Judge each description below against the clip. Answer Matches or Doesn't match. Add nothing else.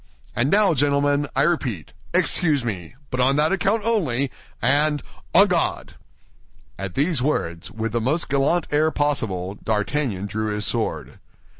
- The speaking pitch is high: Doesn't match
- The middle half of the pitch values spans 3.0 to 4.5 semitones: Doesn't match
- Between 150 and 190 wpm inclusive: Doesn't match